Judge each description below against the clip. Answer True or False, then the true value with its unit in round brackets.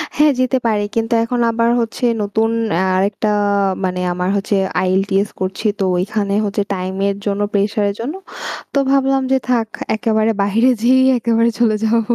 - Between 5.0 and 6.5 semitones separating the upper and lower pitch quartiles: False (2.8 semitones)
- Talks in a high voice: True (220 Hz)